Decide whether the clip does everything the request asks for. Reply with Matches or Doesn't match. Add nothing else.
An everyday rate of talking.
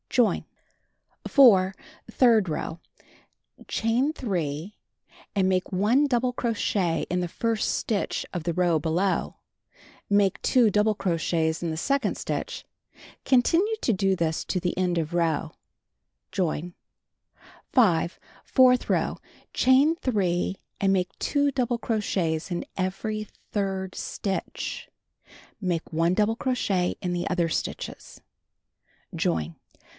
Doesn't match